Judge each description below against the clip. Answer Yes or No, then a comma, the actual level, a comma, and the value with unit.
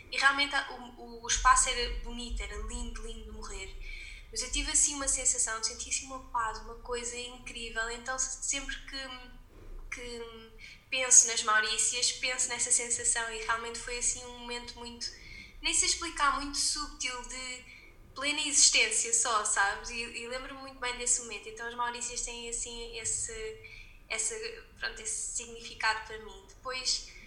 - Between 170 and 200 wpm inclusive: No, average, 160 wpm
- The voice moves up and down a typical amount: No, narrow, 2.1 semitones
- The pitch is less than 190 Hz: No, high, 245 Hz